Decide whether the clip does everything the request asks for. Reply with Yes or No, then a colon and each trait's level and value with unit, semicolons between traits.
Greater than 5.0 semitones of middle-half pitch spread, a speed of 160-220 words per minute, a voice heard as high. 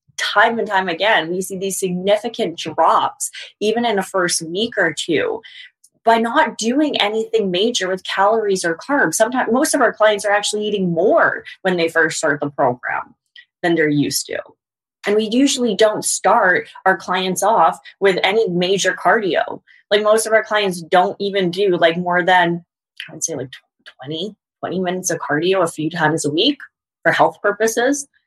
No: average, 3.8 semitones; average, 180 wpm; high, 195 Hz